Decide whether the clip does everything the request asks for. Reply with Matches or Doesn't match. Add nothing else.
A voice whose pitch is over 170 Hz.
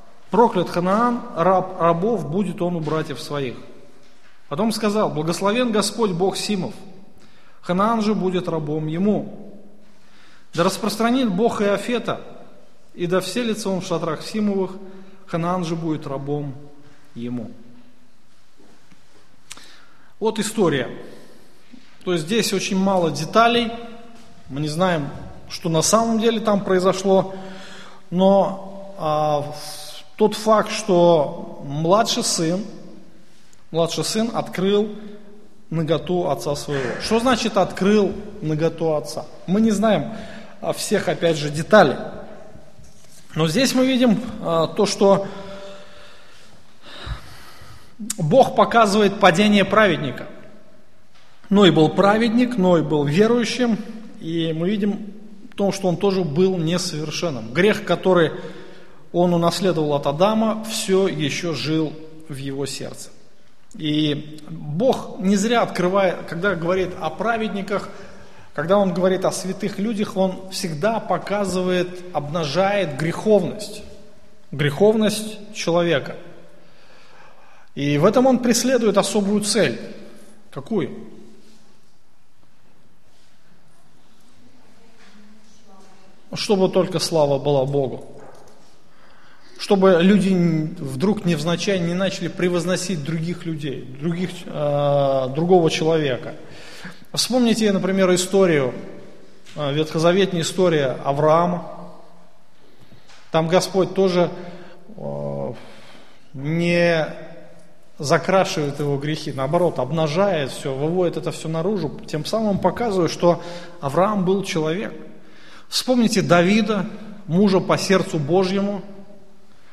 Matches